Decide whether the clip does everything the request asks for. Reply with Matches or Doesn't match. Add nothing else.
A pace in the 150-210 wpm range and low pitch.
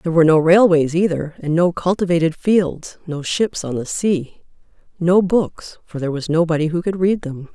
Doesn't match